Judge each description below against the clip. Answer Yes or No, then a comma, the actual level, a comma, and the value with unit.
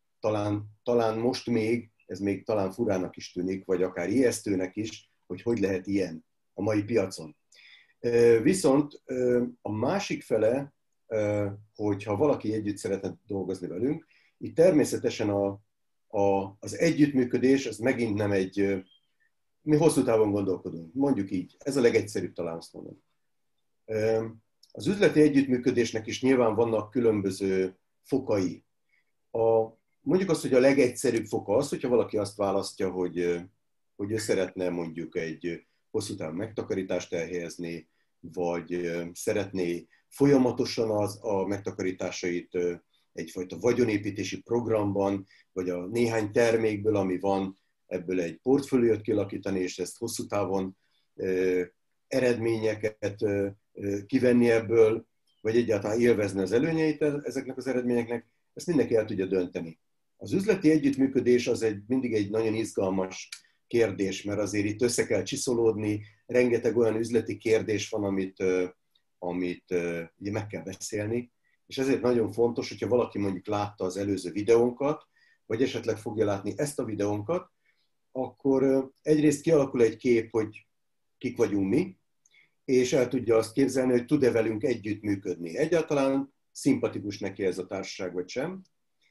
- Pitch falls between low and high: No, low, 105 Hz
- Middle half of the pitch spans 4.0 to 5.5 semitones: Yes, average, 4.3 semitones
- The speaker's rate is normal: Yes, average, 130 wpm